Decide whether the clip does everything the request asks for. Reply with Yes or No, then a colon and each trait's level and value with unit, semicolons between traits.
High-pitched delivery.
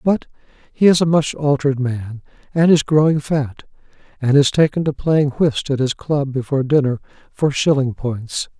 No: medium, 140 Hz